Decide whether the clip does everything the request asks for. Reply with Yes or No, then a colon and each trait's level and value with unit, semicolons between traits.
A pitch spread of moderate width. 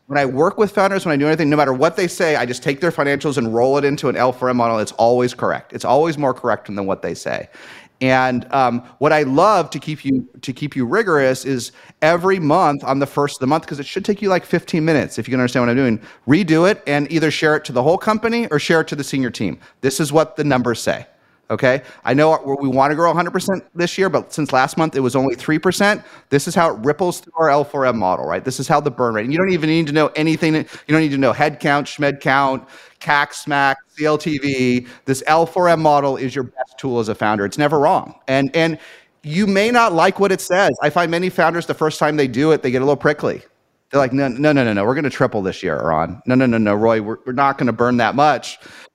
Yes: average, 3.8 semitones